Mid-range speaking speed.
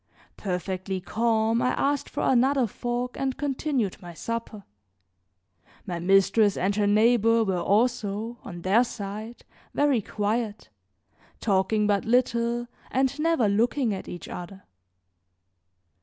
No: slow, 120 wpm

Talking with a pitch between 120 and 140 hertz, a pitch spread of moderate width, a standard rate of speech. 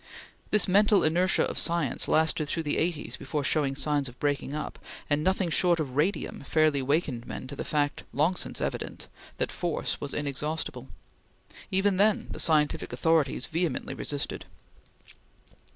No: medium, 155 Hz; average, 3.2 semitones; average, 150 wpm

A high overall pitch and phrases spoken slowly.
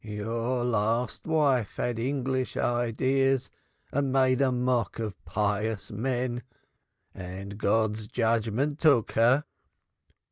No: low, 120 Hz; slow, 100 wpm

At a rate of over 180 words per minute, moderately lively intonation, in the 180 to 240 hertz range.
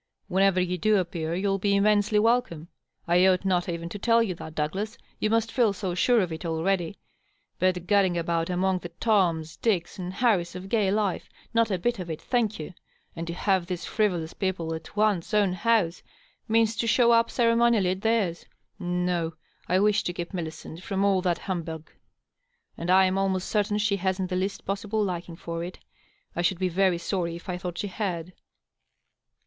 Yes: average, 195 wpm; average, 3.2 semitones; medium, 185 Hz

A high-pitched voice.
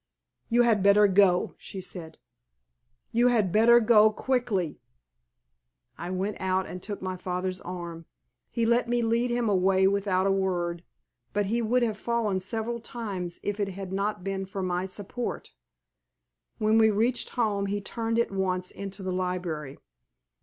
Yes: high, 200 Hz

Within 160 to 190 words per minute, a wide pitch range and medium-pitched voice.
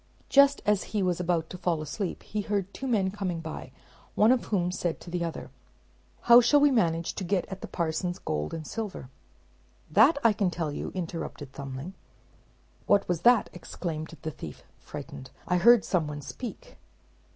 No: average, 180 wpm; average, 4.5 semitones; medium, 180 Hz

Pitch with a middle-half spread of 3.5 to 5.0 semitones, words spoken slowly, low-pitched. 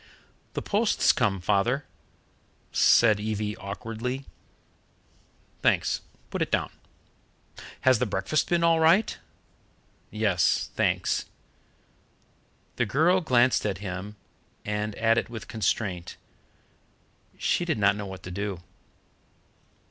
Yes: average, 4.7 semitones; slow, 110 wpm; low, 110 Hz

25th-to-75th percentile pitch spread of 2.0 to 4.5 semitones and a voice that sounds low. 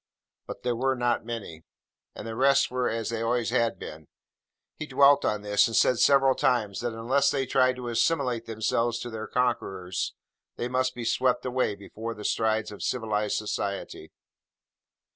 Yes: average, 2.7 semitones; low, 115 Hz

